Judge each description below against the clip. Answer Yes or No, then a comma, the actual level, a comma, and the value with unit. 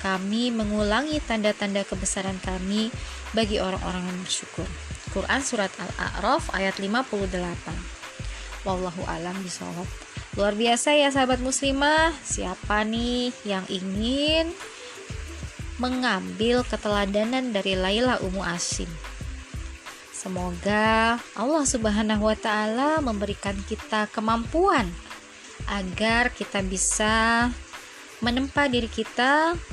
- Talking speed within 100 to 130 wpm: No, average, 90 wpm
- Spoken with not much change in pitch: No, average, 4.1 semitones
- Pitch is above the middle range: Yes, high, 215 Hz